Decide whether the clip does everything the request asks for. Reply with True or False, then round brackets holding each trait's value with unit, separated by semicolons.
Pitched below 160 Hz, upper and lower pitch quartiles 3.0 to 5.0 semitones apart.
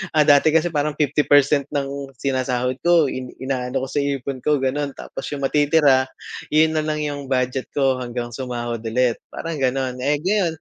False (140 Hz; 2.6 semitones)